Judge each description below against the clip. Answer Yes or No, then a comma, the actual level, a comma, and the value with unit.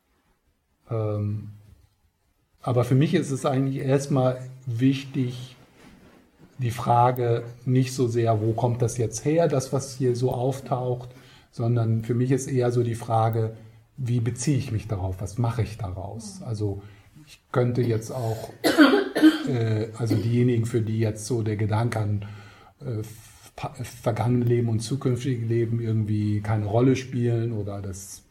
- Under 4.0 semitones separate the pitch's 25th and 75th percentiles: Yes, average, 2.8 semitones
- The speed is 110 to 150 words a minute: Yes, average, 145 wpm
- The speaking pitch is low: Yes, low, 115 Hz